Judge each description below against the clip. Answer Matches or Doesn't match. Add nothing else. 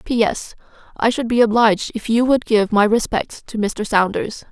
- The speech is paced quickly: Doesn't match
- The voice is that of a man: Doesn't match